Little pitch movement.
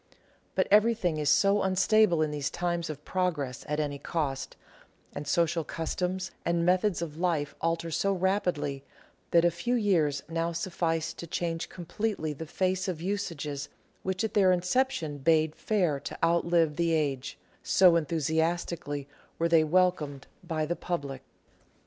No: average, 3.2 semitones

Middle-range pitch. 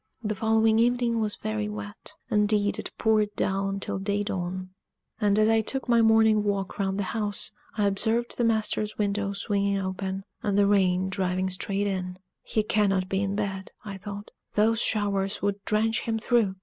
No: high, 205 Hz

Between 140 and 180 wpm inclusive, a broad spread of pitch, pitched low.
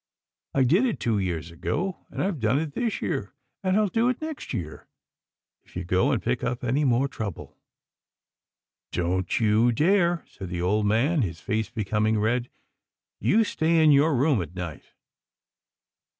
Yes: average, 175 wpm; wide, 8.2 semitones; low, 120 Hz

